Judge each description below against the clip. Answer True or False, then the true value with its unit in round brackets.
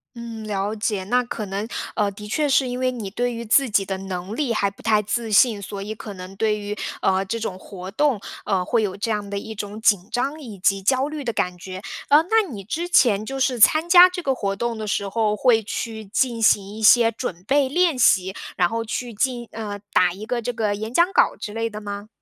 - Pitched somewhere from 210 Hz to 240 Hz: True (220 Hz)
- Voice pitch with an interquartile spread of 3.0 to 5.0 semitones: True (3.6 semitones)